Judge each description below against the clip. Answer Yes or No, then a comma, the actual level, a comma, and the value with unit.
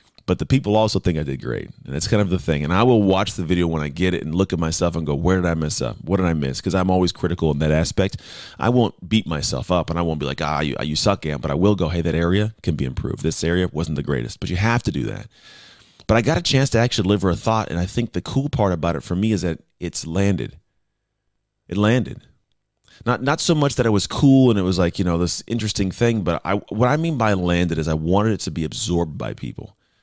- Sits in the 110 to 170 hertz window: No, very low, 95 Hz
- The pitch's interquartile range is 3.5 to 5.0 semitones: Yes, average, 4.5 semitones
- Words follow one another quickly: Yes, fast, 280 wpm